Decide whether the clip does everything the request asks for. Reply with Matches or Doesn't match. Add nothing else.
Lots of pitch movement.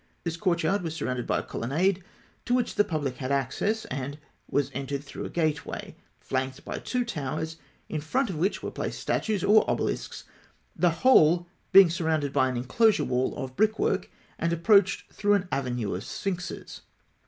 Matches